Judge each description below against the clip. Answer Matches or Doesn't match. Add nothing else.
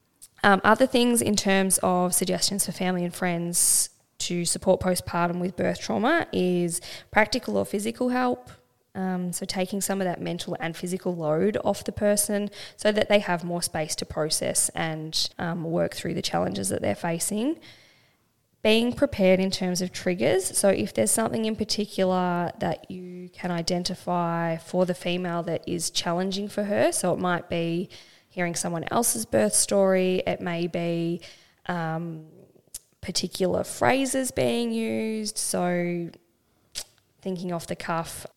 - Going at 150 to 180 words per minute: Matches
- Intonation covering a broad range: Doesn't match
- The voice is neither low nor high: Matches